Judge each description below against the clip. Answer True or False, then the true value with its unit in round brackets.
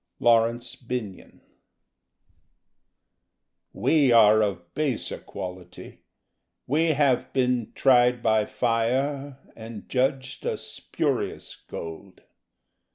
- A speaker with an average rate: False (90 wpm)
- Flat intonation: False (3.5 semitones)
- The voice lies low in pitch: True (120 Hz)